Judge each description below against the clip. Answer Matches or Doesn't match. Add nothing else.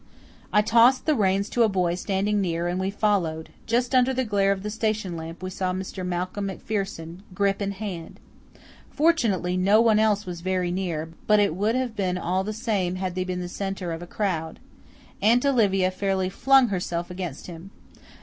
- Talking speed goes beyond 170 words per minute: Matches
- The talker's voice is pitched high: Matches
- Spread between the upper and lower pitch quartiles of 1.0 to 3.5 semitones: Matches